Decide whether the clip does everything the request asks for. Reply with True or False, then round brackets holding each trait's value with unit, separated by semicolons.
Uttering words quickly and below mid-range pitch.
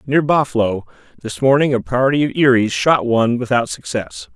False (180 wpm; 120 Hz)